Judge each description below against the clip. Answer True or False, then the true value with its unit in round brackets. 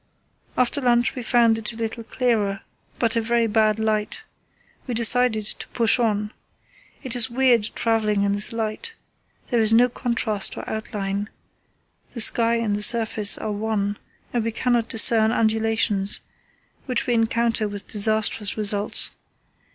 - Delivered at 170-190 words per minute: False (150 wpm)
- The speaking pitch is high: True (225 Hz)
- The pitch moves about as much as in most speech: False (1.9 semitones)